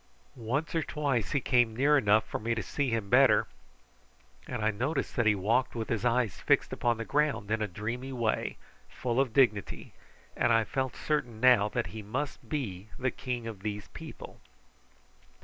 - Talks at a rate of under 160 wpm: No, average, 185 wpm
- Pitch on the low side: Yes, low, 120 Hz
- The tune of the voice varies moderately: Yes, average, 3.4 semitones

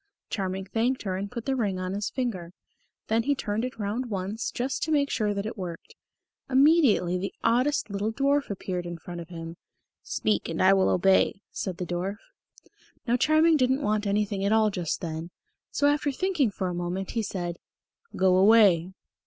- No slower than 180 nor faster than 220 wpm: Yes, average, 185 wpm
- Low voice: No, high, 205 Hz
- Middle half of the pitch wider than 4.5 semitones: Yes, average, 5.2 semitones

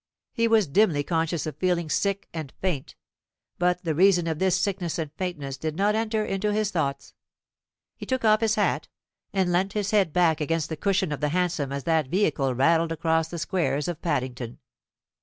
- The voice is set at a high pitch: No, medium, 170 Hz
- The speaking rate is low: No, average, 190 wpm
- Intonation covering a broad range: No, average, 4.2 semitones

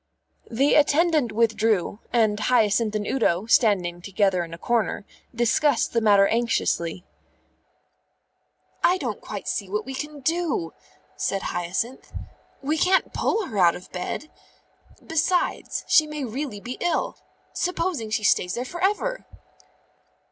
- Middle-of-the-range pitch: No, high, 230 Hz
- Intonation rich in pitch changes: Yes, wide, 6.9 semitones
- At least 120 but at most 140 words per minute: Yes, slow, 135 wpm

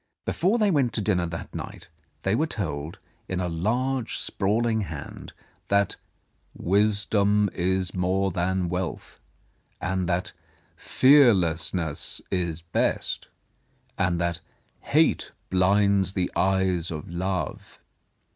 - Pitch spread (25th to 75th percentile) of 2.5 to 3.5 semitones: Yes, average, 3.1 semitones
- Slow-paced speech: Yes, slow, 115 wpm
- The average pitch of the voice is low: Yes, very low, 95 Hz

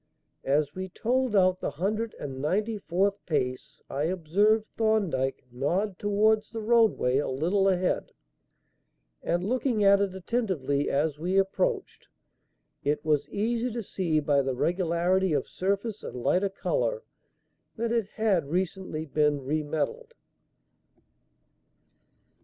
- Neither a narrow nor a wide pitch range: No, wide, 6.0 semitones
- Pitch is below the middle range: No, medium, 185 Hz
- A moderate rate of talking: No, slow, 130 wpm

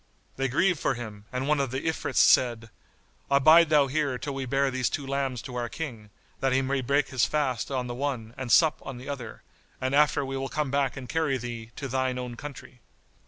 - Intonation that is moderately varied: No, narrow, 2.3 semitones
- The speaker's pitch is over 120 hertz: Yes, low, 135 Hz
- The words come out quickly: Yes, fast, 220 wpm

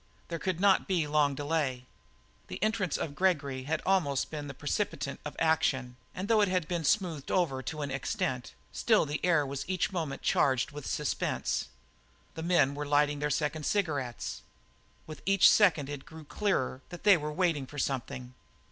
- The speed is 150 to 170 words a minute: No, average, 180 wpm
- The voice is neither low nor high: Yes, medium, 150 Hz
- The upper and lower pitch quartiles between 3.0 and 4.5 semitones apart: Yes, average, 4.2 semitones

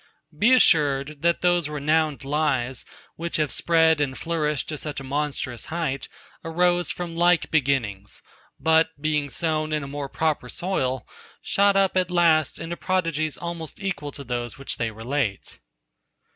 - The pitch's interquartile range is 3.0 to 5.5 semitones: Yes, average, 3.6 semitones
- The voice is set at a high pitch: No, medium, 155 Hz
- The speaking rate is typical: Yes, average, 150 wpm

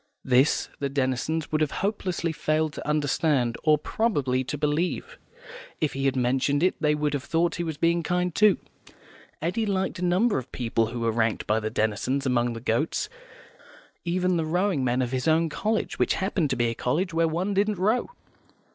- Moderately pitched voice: Yes, medium, 155 Hz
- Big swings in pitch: Yes, wide, 5.7 semitones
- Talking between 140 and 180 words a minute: No, average, 190 wpm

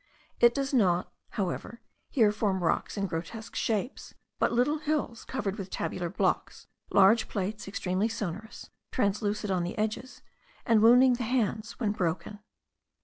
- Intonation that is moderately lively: Yes, average, 3.5 semitones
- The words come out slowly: No, average, 145 wpm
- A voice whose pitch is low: No, high, 215 Hz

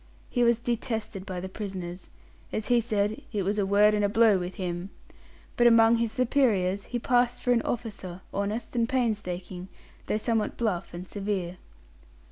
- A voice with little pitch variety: No, average, 3.7 semitones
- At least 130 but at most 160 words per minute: No, average, 170 wpm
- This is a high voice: Yes, high, 210 Hz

